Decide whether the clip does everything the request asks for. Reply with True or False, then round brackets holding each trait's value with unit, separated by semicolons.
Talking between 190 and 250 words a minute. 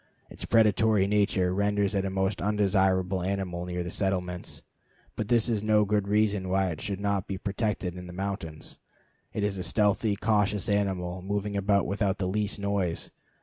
False (170 wpm)